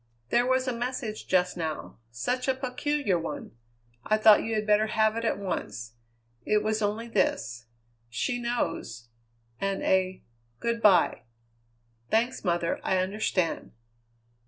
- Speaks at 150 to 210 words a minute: No, slow, 135 wpm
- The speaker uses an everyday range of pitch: Yes, average, 4.4 semitones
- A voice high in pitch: Yes, high, 215 Hz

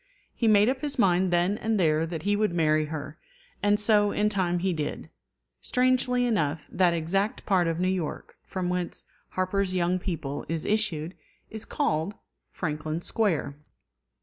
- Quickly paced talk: No, average, 160 wpm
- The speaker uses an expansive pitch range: No, average, 4.2 semitones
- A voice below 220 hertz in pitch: Yes, medium, 185 Hz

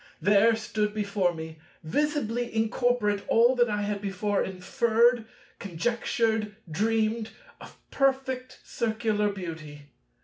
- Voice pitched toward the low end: No, high, 215 Hz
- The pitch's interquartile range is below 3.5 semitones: Yes, average, 2.8 semitones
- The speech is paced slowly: Yes, slow, 105 wpm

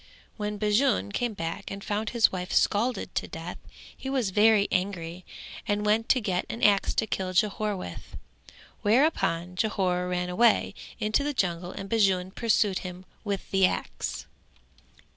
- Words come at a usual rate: Yes, average, 155 wpm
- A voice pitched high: Yes, high, 200 Hz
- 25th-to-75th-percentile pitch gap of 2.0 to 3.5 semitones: Yes, average, 3.2 semitones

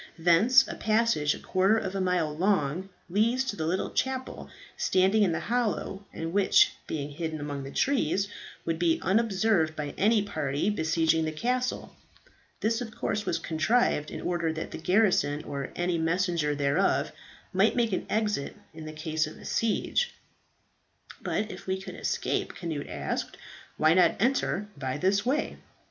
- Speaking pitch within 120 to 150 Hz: No, medium, 185 Hz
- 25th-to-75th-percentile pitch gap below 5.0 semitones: No, average, 5.3 semitones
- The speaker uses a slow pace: No, average, 160 wpm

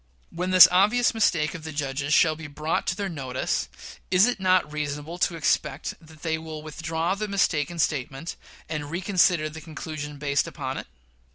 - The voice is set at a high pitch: No, medium, 160 Hz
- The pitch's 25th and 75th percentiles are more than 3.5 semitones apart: No, average, 3.2 semitones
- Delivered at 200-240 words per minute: No, average, 175 wpm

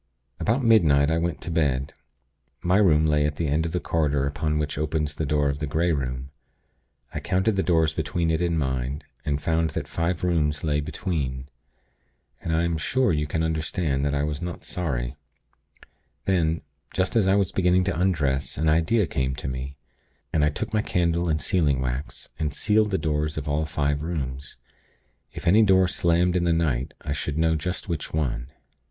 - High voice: No, very low, 80 Hz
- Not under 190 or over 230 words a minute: Yes, average, 195 wpm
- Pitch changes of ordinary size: Yes, average, 3.2 semitones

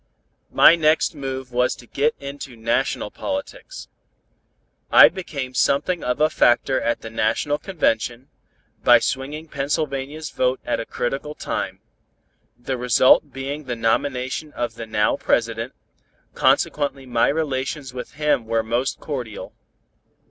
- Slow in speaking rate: Yes, slow, 130 wpm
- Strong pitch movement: No, average, 3.4 semitones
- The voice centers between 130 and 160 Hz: Yes, low, 135 Hz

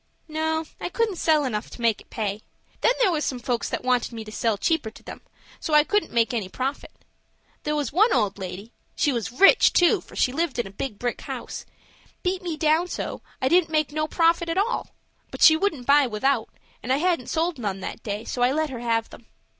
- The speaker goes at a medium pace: No, fast, 225 wpm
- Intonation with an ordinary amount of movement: No, wide, 5.9 semitones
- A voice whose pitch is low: No, very high, 275 Hz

